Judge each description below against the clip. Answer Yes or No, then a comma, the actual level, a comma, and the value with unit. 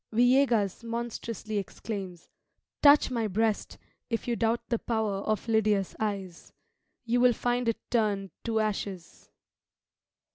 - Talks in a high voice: Yes, high, 220 Hz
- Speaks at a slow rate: Yes, slow, 120 wpm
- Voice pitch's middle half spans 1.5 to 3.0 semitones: Yes, average, 2.7 semitones